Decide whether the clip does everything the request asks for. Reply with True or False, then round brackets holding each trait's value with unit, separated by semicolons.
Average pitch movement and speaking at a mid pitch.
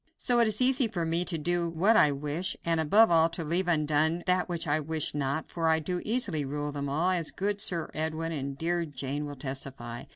True (3.4 semitones; 165 Hz)